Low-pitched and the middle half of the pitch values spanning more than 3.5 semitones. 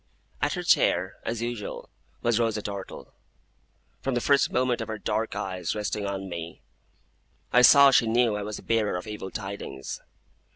No: low, 110 Hz; average, 3.1 semitones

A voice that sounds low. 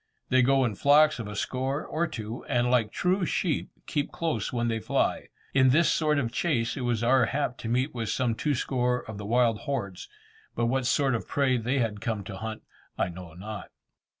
Yes: low, 125 Hz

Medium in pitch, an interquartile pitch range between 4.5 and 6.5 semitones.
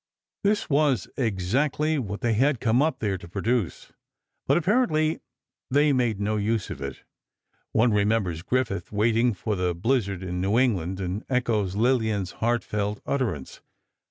No: low, 110 Hz; average, 4.9 semitones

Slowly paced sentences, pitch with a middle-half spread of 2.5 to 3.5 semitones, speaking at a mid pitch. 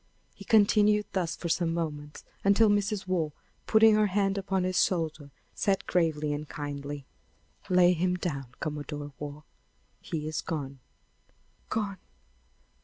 No: slow, 130 wpm; average, 4.8 semitones; medium, 170 Hz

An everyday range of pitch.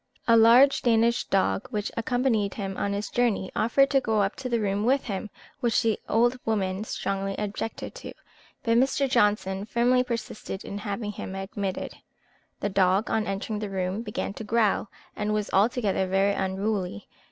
Yes: average, 3.1 semitones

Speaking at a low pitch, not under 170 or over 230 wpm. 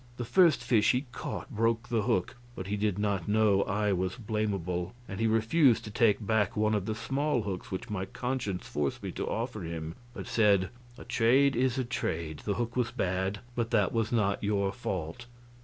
Yes: low, 105 Hz; average, 200 wpm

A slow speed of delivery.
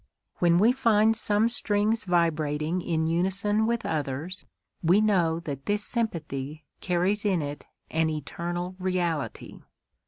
Yes: slow, 125 wpm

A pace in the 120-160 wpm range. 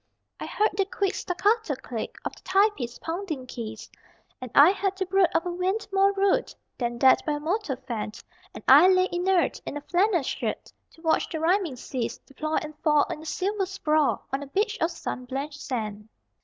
No: average, 195 wpm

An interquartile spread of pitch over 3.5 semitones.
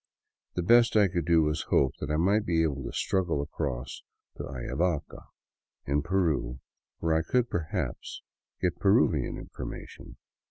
Yes: average, 4.1 semitones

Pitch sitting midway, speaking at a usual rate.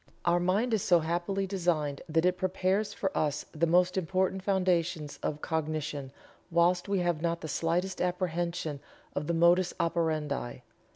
Yes: medium, 175 Hz; average, 155 wpm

